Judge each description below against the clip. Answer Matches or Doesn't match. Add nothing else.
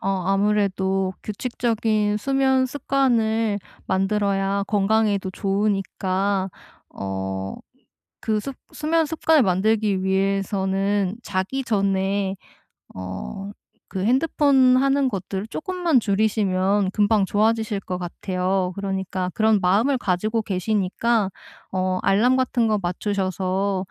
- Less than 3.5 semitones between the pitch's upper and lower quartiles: Matches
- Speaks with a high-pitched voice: Matches